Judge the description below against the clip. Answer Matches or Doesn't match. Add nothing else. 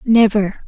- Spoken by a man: Doesn't match